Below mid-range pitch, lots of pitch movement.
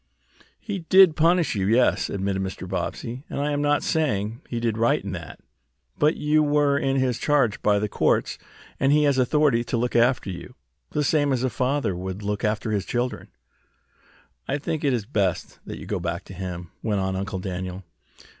Yes: low, 120 Hz; wide, 6.6 semitones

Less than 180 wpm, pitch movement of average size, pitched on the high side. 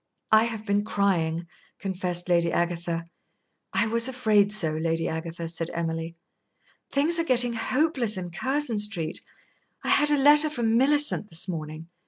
No: average, 150 wpm; wide, 6.6 semitones; high, 200 Hz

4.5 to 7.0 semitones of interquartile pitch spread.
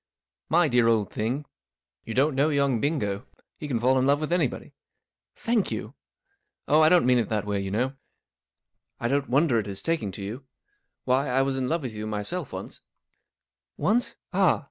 Yes: wide, 5.6 semitones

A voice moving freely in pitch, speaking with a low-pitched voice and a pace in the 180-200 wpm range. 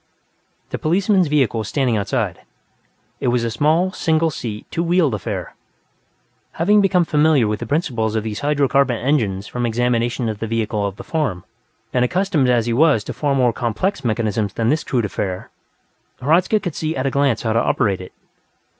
Yes: wide, 5.8 semitones; low, 125 Hz; average, 185 wpm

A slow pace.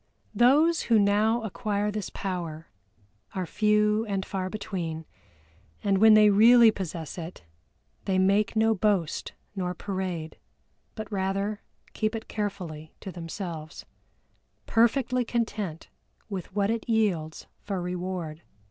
Yes: slow, 120 wpm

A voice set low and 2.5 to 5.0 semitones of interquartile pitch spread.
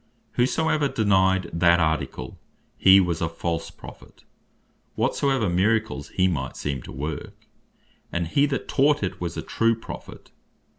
No: very low, 95 Hz; wide, 5.6 semitones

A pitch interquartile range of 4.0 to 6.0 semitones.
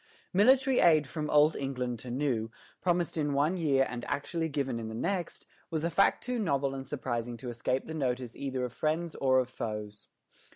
Yes: average, 4.6 semitones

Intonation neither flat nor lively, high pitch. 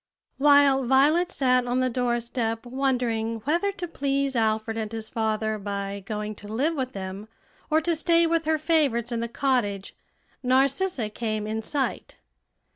Yes: average, 4.4 semitones; high, 245 Hz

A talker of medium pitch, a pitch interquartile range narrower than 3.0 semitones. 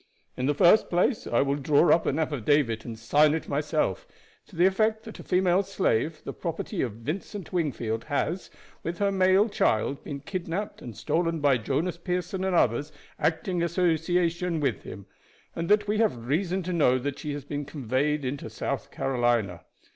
No: medium, 160 Hz; average, 5.0 semitones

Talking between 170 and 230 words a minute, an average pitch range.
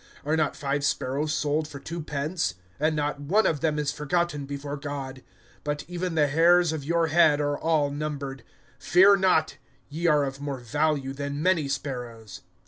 No: average, 175 wpm; narrow, 2.2 semitones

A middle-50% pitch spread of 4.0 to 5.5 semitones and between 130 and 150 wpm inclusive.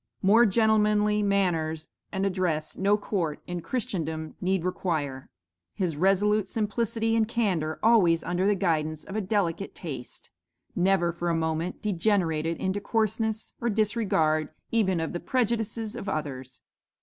Yes: average, 4.5 semitones; slow, 135 wpm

